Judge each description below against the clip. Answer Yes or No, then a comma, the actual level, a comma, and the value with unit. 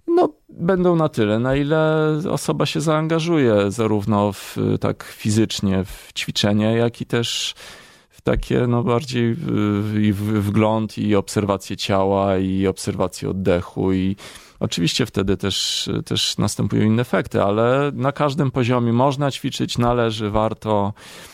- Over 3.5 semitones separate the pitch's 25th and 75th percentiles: Yes, average, 4.1 semitones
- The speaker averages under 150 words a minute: Yes, average, 130 wpm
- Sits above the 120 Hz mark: No, low, 110 Hz